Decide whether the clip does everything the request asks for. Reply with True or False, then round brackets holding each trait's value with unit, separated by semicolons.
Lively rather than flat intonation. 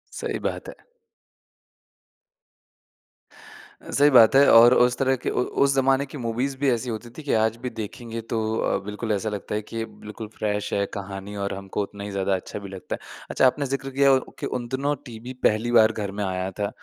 False (4.1 semitones)